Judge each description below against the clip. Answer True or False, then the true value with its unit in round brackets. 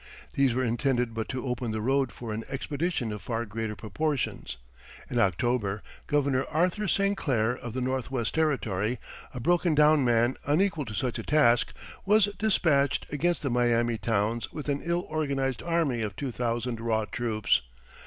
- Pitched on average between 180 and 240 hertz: False (125 Hz)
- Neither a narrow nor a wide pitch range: True (4.4 semitones)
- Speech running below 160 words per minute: False (165 wpm)